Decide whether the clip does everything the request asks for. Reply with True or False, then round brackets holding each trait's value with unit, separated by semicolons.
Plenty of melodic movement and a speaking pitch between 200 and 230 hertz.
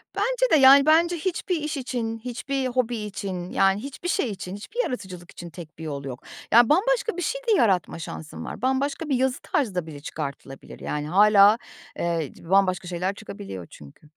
True (8.1 semitones; 215 Hz)